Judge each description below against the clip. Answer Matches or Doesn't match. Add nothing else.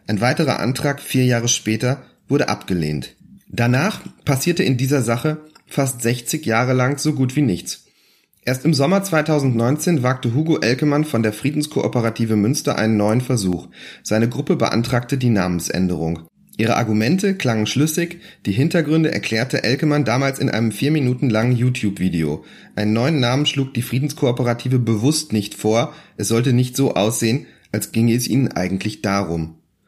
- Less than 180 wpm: Matches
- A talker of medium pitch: Doesn't match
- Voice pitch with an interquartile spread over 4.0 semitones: Matches